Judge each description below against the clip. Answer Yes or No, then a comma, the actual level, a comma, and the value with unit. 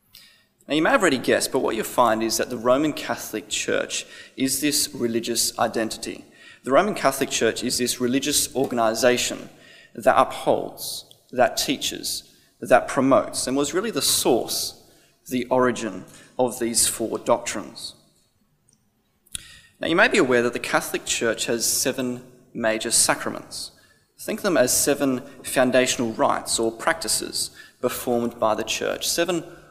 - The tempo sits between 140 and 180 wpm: Yes, average, 145 wpm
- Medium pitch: No, low, 125 Hz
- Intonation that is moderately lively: No, narrow, 2.1 semitones